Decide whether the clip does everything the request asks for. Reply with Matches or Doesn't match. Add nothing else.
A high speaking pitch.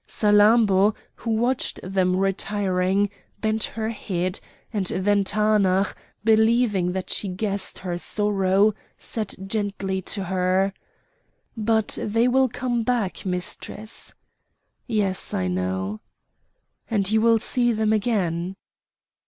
Matches